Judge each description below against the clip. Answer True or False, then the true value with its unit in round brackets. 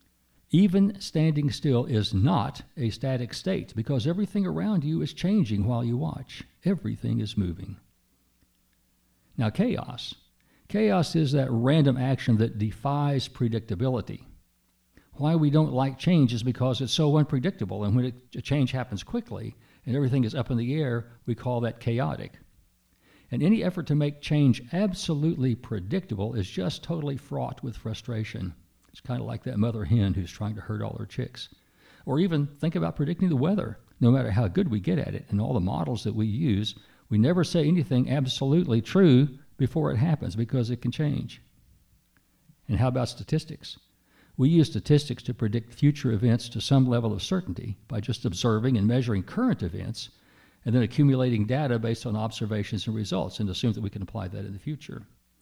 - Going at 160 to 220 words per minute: True (175 wpm)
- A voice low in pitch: True (125 Hz)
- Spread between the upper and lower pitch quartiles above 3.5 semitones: True (4.9 semitones)